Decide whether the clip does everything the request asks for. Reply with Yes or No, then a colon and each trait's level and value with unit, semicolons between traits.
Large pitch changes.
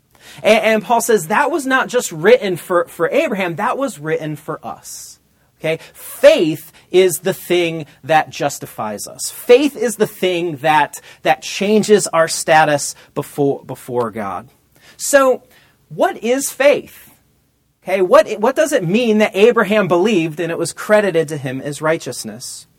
Yes: wide, 6.0 semitones